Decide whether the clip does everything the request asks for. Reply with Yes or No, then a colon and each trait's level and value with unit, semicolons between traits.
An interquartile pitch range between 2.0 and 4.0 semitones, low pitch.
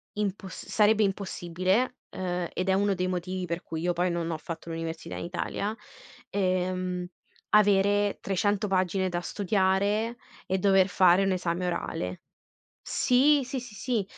No: narrow, 2.4 semitones; high, 190 Hz